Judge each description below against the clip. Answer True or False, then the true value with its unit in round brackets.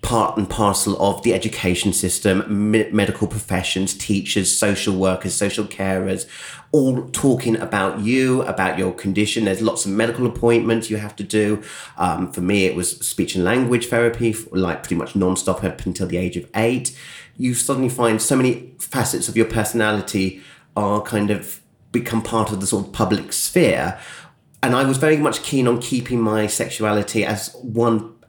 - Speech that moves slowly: False (180 wpm)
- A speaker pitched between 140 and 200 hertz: False (110 Hz)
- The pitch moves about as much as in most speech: True (3.2 semitones)